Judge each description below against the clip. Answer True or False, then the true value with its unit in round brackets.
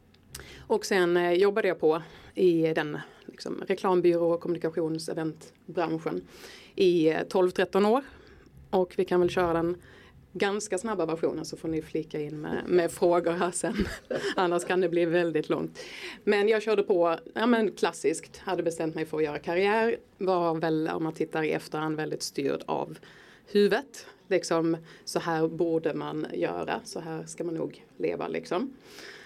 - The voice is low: False (175 Hz)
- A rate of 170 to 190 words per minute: False (160 wpm)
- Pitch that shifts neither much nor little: True (3.2 semitones)